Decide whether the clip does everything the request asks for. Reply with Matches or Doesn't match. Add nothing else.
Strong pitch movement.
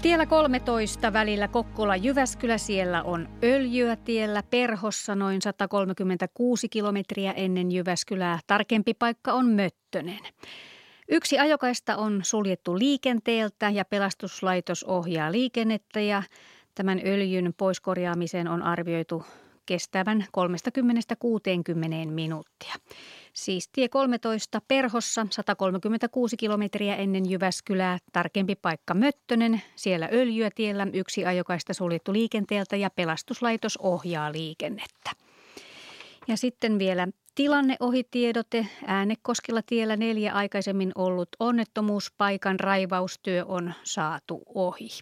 Doesn't match